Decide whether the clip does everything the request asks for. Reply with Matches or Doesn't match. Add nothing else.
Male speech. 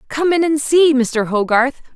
Doesn't match